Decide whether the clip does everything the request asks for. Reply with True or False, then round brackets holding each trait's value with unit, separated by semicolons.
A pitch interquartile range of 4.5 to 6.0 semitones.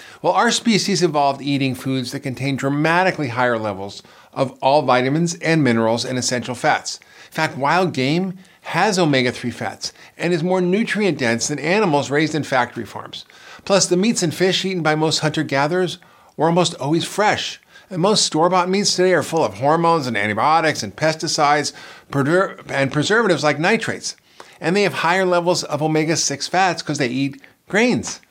True (4.9 semitones)